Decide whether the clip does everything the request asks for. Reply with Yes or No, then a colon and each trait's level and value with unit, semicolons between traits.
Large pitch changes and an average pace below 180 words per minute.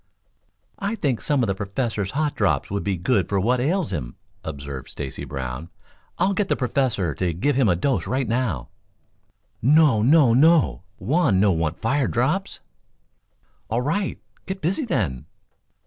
Yes: wide, 8.5 semitones; average, 160 wpm